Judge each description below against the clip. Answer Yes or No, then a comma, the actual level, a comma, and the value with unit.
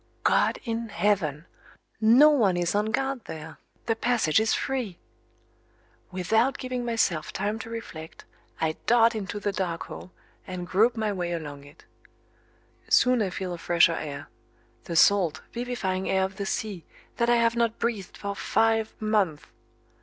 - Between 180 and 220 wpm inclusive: No, average, 155 wpm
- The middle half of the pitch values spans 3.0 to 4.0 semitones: No, average, 4.7 semitones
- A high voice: Yes, high, 205 Hz